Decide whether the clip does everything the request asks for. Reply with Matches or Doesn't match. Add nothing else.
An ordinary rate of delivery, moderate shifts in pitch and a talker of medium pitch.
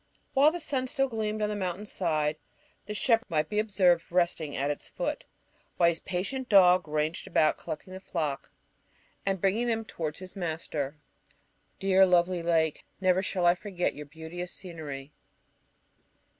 Matches